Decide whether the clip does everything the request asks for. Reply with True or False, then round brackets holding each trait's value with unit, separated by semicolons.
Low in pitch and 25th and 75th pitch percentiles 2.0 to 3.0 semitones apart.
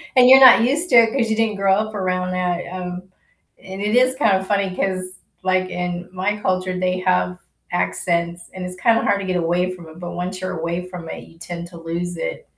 False (185 Hz; 2.6 semitones)